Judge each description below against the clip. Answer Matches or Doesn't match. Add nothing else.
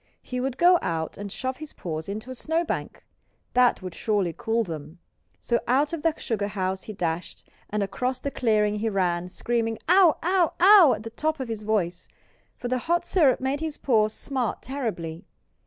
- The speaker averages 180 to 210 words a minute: Matches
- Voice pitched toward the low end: Doesn't match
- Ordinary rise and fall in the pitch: Doesn't match